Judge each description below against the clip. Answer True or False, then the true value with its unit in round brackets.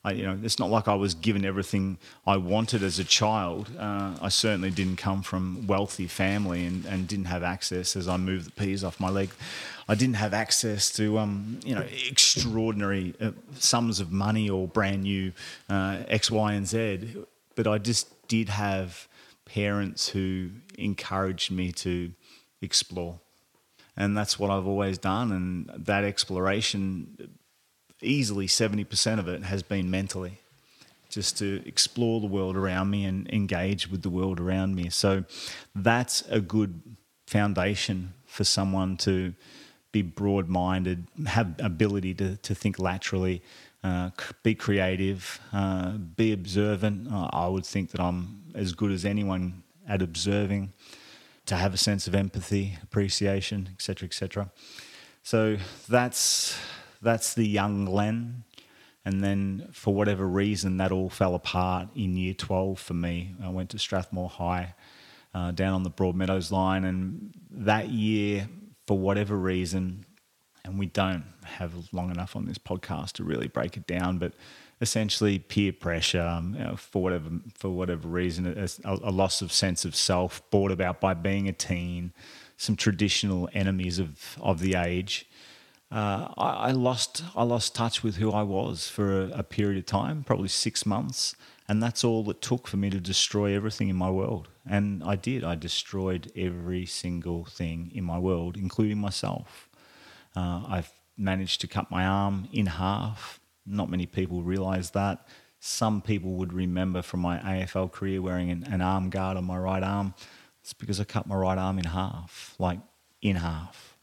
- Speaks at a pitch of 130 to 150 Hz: False (95 Hz)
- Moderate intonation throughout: False (2.1 semitones)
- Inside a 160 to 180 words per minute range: True (165 wpm)